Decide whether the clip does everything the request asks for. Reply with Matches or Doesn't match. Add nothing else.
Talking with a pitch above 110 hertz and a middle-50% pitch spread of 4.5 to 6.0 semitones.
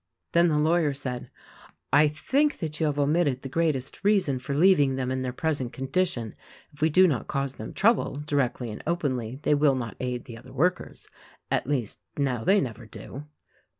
Doesn't match